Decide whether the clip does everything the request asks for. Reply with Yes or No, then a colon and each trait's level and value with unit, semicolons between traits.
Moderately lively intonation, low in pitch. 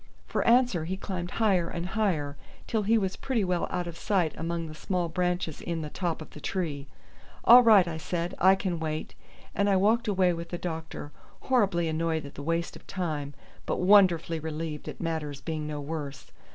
No: average, 3.1 semitones; medium, 170 Hz